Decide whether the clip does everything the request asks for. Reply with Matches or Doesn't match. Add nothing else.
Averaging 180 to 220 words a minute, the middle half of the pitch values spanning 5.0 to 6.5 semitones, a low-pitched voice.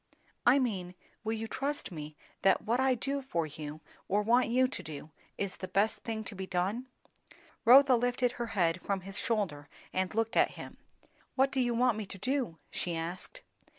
Doesn't match